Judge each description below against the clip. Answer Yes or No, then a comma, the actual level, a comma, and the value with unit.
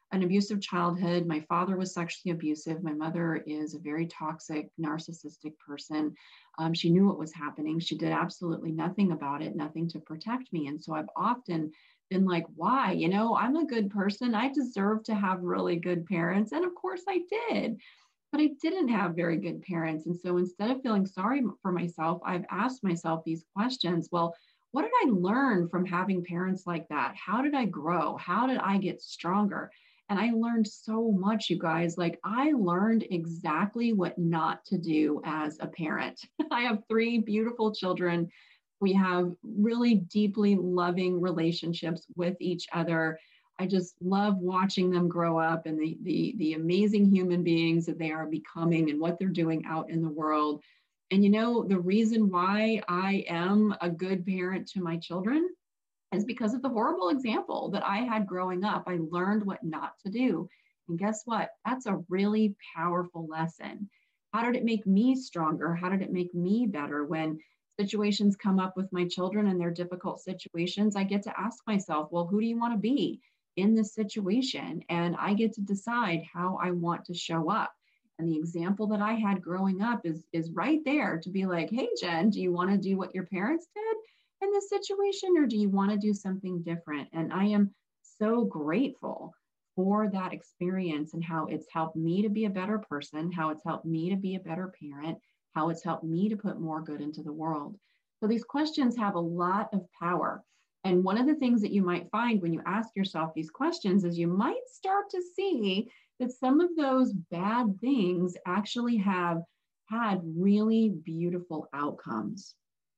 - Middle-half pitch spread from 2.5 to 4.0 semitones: No, average, 4.4 semitones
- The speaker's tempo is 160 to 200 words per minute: Yes, average, 190 wpm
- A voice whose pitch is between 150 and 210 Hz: Yes, medium, 185 Hz